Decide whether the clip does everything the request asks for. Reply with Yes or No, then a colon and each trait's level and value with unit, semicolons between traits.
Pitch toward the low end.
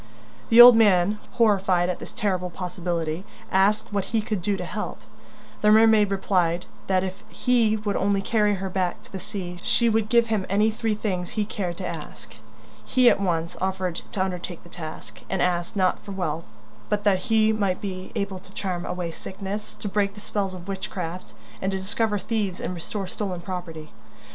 No: high, 190 Hz